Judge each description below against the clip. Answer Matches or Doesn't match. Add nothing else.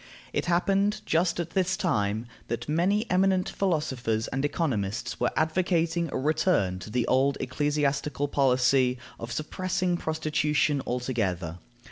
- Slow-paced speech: Matches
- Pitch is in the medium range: Matches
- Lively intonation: Matches